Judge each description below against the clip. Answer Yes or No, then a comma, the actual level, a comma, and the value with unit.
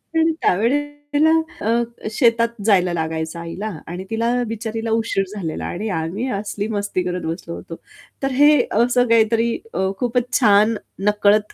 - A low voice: No, high, 220 Hz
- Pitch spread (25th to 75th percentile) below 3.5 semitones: No, average, 4.0 semitones